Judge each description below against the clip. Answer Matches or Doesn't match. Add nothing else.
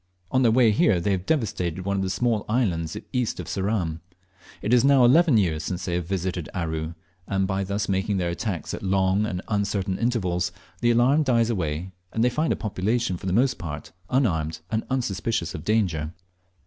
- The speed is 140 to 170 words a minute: Doesn't match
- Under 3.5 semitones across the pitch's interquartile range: Doesn't match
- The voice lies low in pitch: Matches